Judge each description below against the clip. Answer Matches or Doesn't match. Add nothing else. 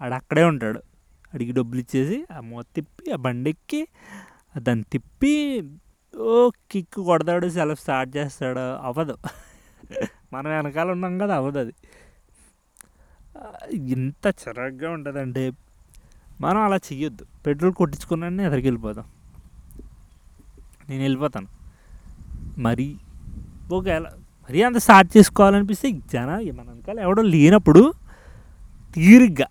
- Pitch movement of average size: Doesn't match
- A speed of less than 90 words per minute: Doesn't match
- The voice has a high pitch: Doesn't match